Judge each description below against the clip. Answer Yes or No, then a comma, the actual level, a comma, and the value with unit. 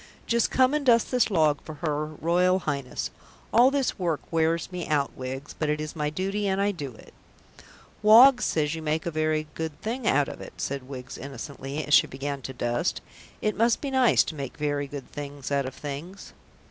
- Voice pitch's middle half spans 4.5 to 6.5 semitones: Yes, wide, 5.6 semitones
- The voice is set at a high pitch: No, medium, 155 Hz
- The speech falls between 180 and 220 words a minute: Yes, fast, 205 wpm